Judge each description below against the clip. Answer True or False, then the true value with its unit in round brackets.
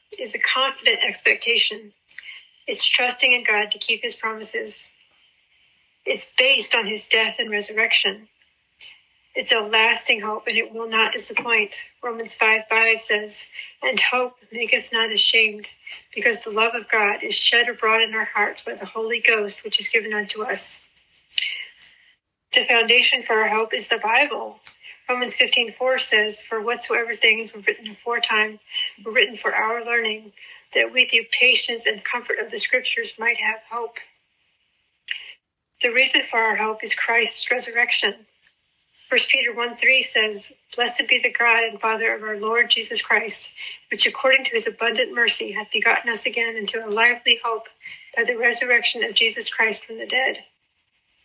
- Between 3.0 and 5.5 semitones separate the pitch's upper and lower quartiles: False (2.6 semitones)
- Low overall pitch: False (230 Hz)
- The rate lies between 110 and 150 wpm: False (165 wpm)